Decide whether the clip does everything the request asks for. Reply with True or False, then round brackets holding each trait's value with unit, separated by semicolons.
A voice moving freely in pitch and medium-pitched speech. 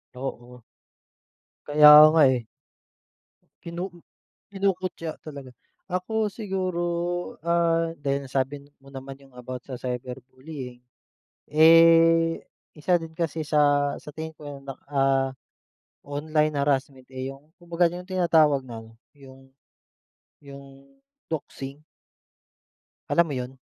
False (3.8 semitones; 145 Hz)